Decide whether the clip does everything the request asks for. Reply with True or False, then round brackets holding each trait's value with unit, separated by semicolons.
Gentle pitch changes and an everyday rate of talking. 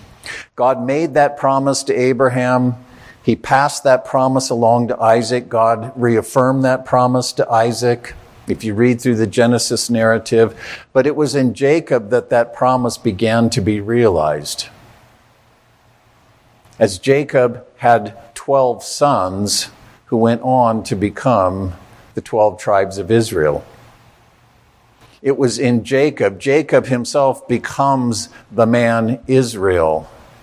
False (2.3 semitones; 125 wpm)